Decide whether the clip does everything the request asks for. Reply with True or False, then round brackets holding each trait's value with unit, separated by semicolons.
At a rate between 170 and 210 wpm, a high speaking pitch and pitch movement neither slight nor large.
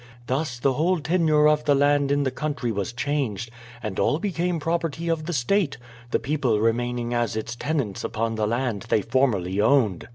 False (190 wpm; 135 Hz; 5.0 semitones)